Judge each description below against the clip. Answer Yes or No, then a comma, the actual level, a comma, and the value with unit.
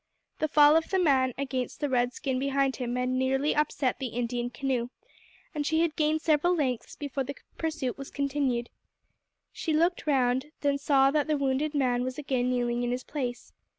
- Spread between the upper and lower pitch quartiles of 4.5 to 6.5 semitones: No, average, 3.0 semitones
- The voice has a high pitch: Yes, very high, 270 Hz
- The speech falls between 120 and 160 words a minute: No, average, 185 wpm